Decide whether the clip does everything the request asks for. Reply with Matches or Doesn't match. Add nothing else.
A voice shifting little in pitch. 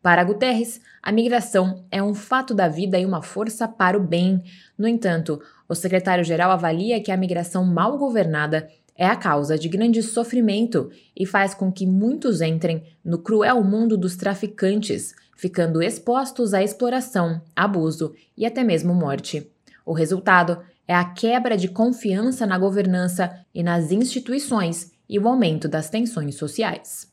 Doesn't match